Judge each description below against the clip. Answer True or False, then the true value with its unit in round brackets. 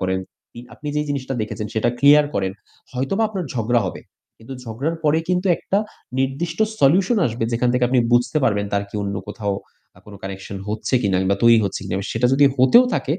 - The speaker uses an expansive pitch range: True (6.0 semitones)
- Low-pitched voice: True (125 Hz)